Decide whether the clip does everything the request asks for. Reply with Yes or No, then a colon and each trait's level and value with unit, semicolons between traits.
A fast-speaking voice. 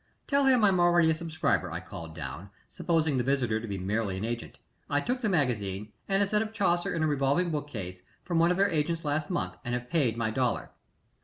Yes: fast, 225 wpm